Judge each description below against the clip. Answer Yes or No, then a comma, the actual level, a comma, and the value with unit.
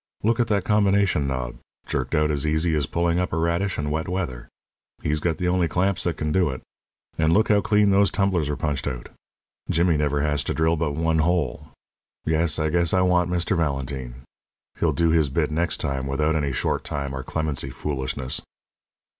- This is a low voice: Yes, very low, 80 Hz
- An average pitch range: Yes, average, 3.6 semitones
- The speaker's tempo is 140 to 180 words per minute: No, average, 195 wpm